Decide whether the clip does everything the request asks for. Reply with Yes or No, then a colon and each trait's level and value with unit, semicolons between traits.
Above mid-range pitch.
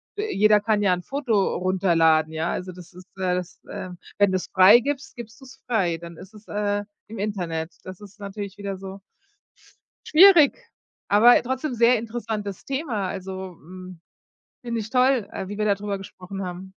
Yes: high, 200 Hz